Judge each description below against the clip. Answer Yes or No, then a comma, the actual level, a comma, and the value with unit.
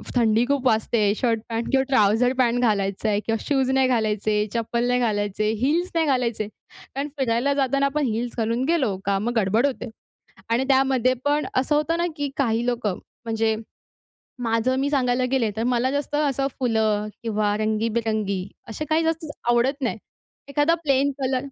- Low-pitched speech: No, high, 245 Hz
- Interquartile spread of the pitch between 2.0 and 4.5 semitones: Yes, average, 3.6 semitones